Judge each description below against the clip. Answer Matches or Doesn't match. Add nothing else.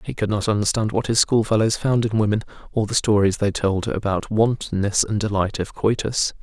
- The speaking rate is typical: Matches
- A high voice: Doesn't match